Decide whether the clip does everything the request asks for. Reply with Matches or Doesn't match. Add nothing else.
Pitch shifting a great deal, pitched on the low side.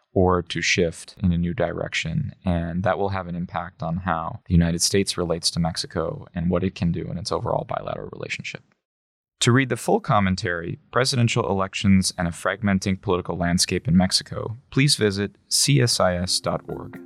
Doesn't match